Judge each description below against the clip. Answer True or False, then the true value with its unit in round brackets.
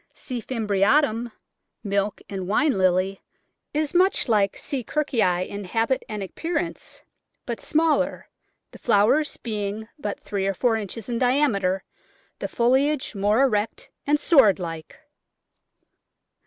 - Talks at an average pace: False (130 wpm)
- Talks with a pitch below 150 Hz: False (220 Hz)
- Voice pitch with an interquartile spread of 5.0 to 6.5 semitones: True (5.3 semitones)